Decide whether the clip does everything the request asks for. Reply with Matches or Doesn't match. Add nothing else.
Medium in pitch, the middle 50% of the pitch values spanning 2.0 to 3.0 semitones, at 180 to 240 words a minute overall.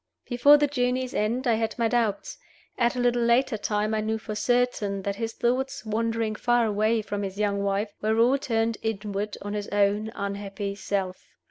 Doesn't match